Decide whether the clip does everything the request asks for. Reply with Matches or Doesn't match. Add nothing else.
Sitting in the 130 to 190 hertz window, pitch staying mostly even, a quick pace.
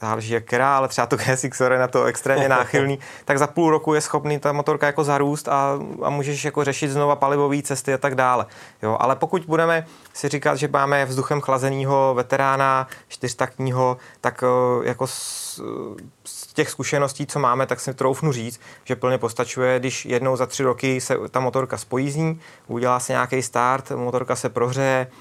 Matches